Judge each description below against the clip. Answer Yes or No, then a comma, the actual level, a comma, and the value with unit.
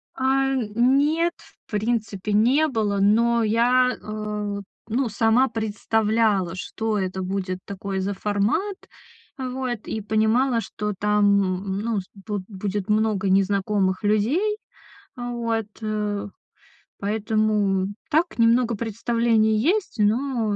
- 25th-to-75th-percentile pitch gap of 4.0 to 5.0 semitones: No, average, 2.9 semitones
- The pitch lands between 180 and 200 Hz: No, high, 215 Hz